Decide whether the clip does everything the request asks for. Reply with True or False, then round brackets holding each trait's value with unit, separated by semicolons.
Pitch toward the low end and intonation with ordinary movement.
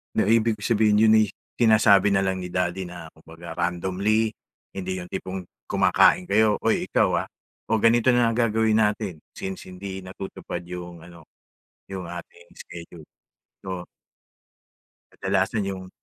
True (95 Hz; 3.4 semitones)